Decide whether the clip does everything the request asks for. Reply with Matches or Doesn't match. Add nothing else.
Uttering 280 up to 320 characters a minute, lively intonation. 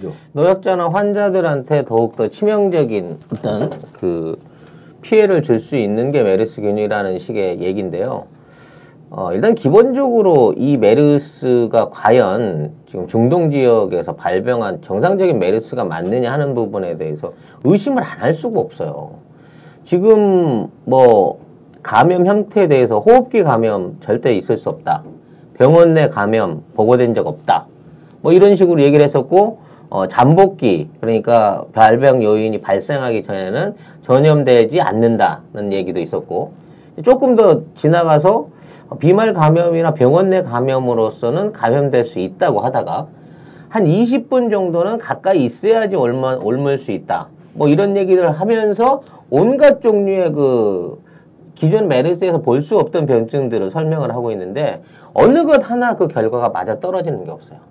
Matches